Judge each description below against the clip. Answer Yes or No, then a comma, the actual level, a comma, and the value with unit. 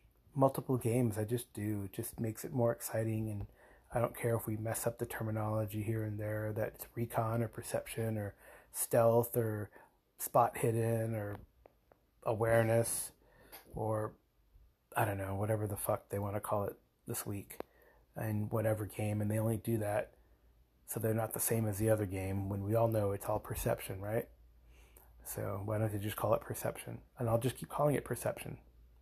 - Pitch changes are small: Yes, narrow, 2.1 semitones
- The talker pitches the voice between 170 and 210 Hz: No, low, 110 Hz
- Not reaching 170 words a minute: No, average, 185 wpm